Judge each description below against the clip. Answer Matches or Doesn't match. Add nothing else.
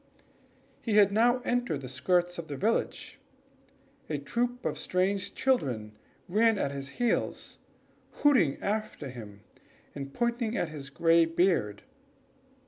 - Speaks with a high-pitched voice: Doesn't match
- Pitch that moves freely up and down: Matches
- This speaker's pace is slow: Matches